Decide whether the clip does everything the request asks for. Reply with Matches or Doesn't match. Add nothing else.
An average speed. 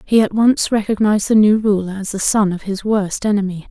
Doesn't match